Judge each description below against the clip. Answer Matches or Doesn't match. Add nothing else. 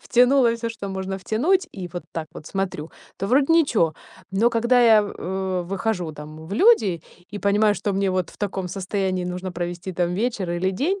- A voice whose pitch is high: Matches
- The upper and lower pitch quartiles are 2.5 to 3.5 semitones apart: Doesn't match